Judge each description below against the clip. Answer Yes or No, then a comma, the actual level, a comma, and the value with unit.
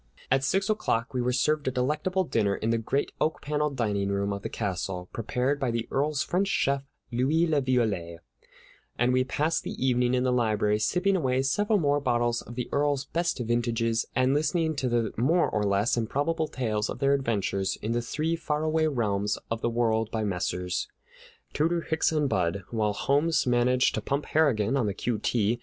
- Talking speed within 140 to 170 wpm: No, average, 190 wpm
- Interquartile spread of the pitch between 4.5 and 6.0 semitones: Yes, average, 4.9 semitones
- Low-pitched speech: Yes, low, 125 Hz